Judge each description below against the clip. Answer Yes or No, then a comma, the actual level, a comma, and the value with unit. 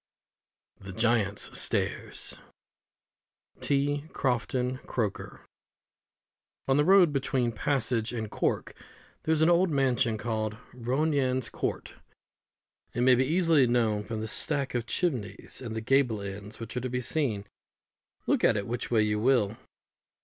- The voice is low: Yes, low, 125 Hz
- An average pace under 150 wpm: Yes, average, 140 wpm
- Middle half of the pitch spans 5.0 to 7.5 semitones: No, average, 3.9 semitones